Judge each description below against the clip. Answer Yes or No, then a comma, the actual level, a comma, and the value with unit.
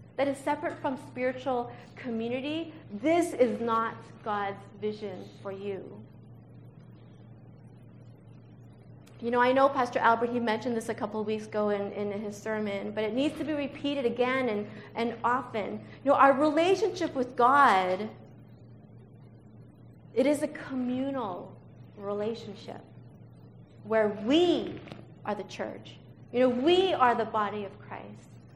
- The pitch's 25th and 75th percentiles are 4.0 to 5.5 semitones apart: Yes, average, 4.7 semitones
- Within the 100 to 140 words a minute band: Yes, slow, 135 wpm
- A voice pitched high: Yes, high, 240 Hz